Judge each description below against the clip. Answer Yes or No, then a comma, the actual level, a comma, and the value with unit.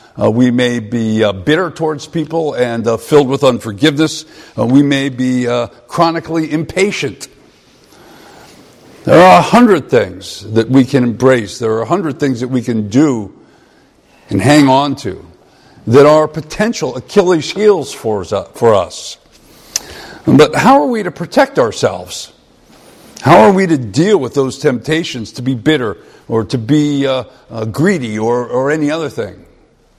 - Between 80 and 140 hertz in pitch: Yes, low, 135 Hz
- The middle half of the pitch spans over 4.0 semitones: Yes, average, 4.6 semitones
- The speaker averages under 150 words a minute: No, average, 160 wpm